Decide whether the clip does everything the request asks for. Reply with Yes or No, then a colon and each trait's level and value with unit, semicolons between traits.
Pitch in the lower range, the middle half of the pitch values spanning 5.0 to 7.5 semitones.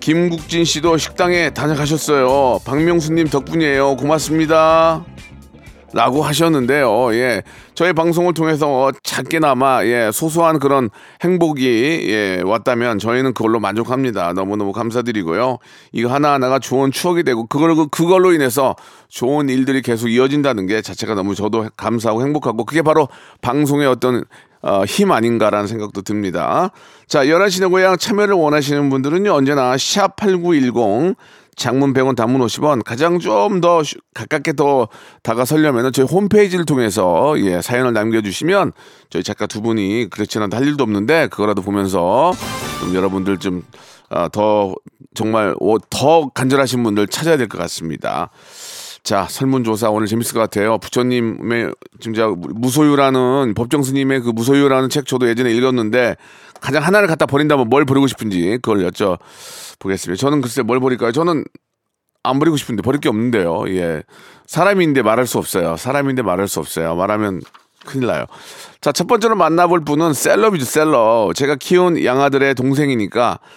Yes: low, 130 Hz; wide, 5.6 semitones